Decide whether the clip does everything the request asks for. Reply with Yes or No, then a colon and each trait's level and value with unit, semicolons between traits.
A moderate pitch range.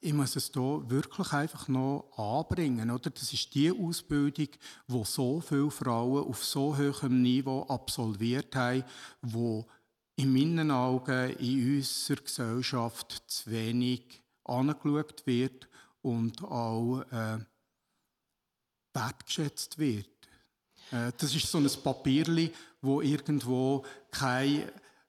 Yes: average, 3.0 semitones